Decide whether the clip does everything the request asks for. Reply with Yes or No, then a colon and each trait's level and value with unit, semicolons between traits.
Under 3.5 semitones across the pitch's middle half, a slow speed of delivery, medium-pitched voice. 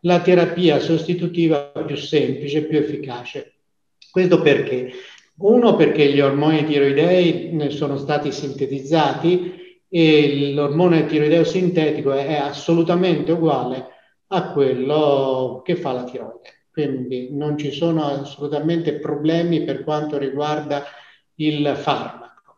Yes: average, 2.8 semitones; slow, 110 wpm; medium, 150 Hz